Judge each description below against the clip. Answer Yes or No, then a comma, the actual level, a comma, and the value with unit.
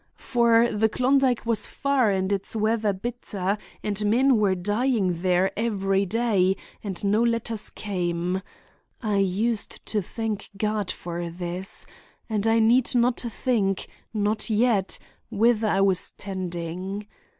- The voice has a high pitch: Yes, high, 210 Hz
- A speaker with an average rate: No, slow, 125 wpm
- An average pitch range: Yes, average, 3.3 semitones